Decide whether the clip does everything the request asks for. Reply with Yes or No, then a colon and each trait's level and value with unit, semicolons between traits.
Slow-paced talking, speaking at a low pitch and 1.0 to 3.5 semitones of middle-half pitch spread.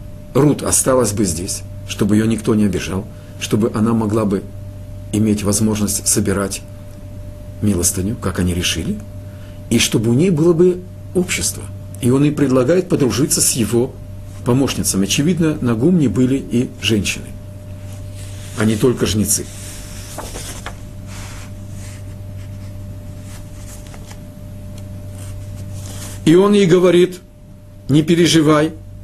Yes: slow, 105 wpm; low, 100 Hz; average, 3.0 semitones